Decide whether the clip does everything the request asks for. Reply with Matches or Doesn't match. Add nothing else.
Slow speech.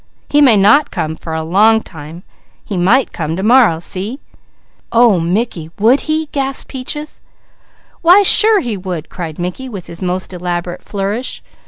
Doesn't match